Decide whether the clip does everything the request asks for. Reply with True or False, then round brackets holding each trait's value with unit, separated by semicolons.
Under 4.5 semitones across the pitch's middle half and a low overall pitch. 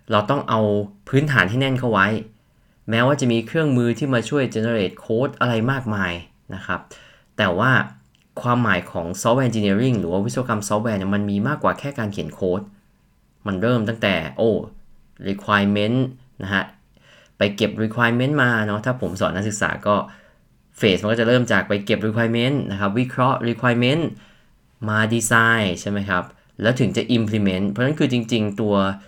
True (3.4 semitones; 110 Hz)